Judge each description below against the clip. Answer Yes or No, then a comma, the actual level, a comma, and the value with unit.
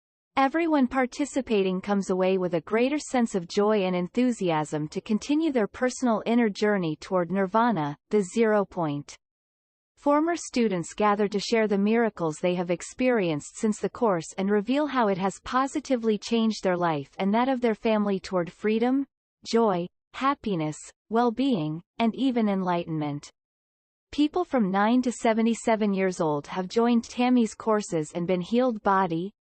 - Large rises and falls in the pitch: No, average, 4.9 semitones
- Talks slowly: Yes, slow, 150 wpm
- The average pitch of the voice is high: Yes, high, 210 Hz